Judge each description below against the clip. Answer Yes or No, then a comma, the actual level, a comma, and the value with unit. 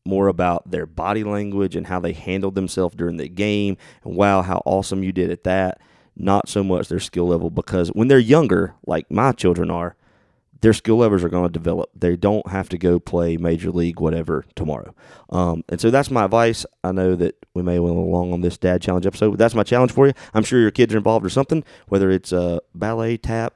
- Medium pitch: No, very low, 95 Hz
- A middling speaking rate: No, fast, 230 wpm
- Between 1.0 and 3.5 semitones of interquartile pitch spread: No, average, 4.0 semitones